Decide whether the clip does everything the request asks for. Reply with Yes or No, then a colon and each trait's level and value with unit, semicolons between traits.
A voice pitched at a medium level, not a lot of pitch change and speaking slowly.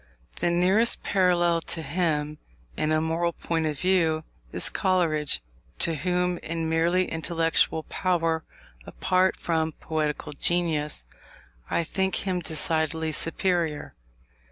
Yes: medium, 165 Hz; narrow, 2.1 semitones; slow, 115 wpm